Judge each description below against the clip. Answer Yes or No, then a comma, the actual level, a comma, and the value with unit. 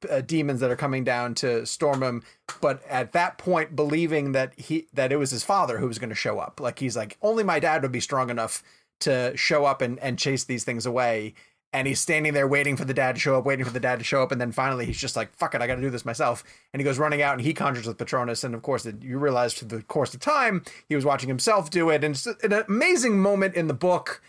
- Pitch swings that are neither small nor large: Yes, average, 3.5 semitones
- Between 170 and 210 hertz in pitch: No, low, 135 Hz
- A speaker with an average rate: No, fast, 275 wpm